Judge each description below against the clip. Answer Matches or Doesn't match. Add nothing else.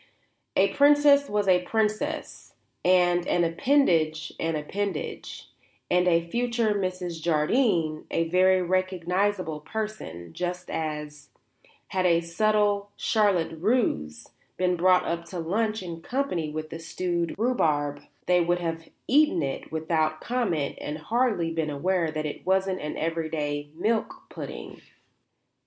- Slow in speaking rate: Matches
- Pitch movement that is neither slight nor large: Matches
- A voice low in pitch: Doesn't match